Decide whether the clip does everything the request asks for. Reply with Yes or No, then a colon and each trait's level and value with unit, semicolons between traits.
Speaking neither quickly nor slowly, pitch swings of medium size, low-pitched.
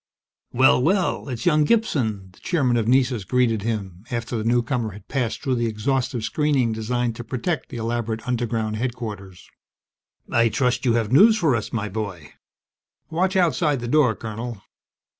Yes: average, 160 wpm; average, 3.2 semitones; low, 120 Hz